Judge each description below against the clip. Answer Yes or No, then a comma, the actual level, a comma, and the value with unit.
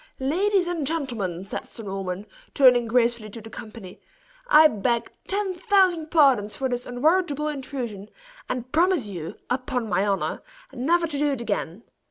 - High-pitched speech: Yes, very high, 250 Hz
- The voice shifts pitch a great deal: Yes, wide, 6.6 semitones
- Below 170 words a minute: Yes, average, 155 wpm